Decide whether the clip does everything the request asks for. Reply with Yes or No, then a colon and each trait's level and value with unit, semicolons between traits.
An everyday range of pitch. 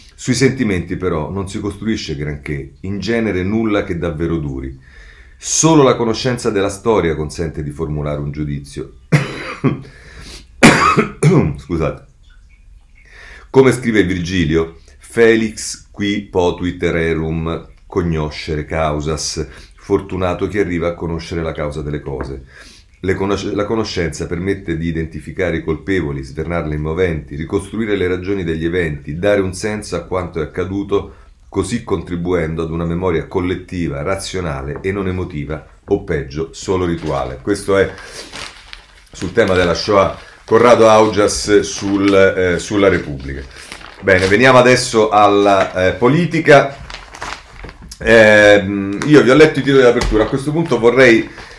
Yes: average, 4.4 semitones